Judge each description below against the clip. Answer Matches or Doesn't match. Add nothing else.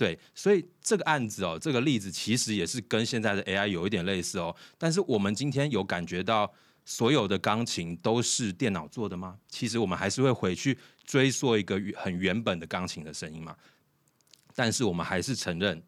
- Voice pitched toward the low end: Matches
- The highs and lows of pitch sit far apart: Matches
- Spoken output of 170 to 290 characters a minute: Doesn't match